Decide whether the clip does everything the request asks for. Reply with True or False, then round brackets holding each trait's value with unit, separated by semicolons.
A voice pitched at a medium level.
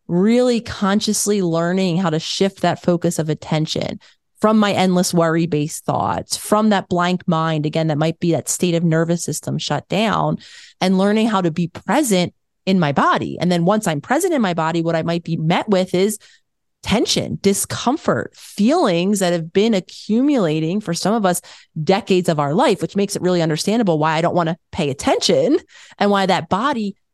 True (180 Hz)